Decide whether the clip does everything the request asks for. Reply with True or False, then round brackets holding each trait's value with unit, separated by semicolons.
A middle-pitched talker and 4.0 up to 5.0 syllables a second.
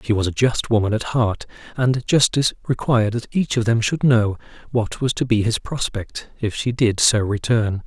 False (115 Hz; 4.9 syllables/s)